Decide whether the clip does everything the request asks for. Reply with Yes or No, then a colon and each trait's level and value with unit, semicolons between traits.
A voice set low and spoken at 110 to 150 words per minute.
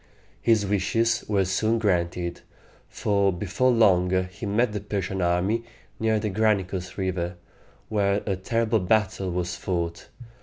Yes: low, 100 Hz; average, 140 wpm